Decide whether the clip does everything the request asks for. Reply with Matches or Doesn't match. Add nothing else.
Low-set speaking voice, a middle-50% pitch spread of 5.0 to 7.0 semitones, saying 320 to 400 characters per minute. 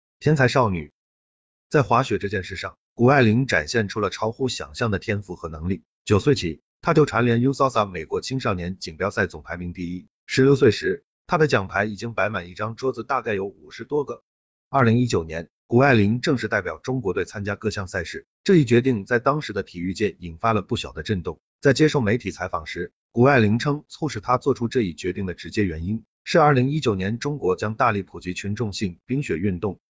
Matches